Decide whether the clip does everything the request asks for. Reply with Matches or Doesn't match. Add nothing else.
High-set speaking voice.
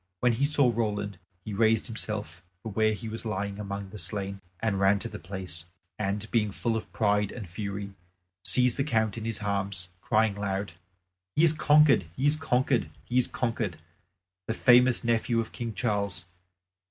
Doesn't match